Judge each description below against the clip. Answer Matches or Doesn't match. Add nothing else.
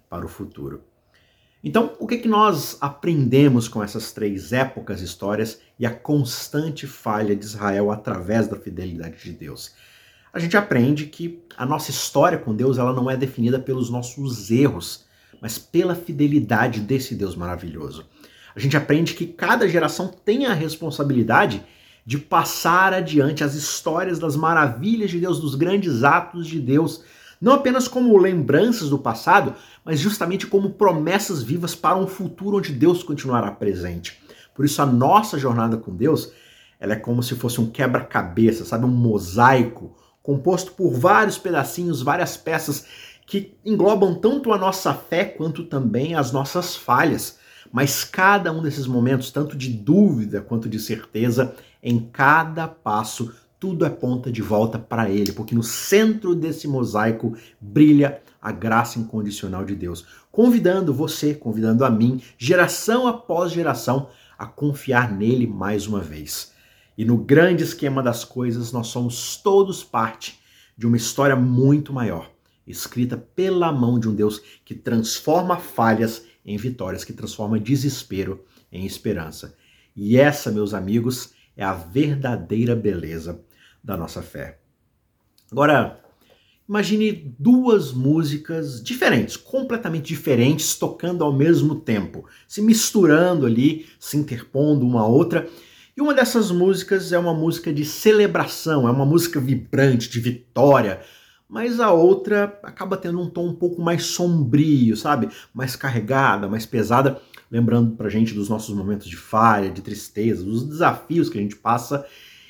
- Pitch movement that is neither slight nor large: Doesn't match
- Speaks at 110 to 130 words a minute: Doesn't match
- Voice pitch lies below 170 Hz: Matches